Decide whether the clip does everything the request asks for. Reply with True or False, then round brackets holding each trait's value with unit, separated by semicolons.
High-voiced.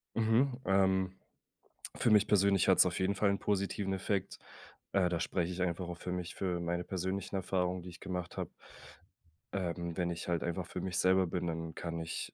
False (90 Hz)